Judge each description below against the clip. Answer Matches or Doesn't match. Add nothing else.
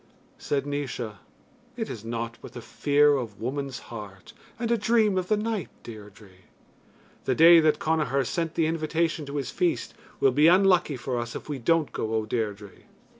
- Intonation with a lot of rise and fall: Matches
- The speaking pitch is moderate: Matches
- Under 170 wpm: Doesn't match